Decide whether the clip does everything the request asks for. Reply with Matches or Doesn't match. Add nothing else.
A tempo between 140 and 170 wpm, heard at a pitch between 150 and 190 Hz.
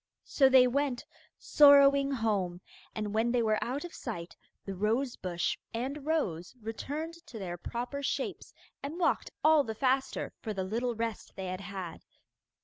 Doesn't match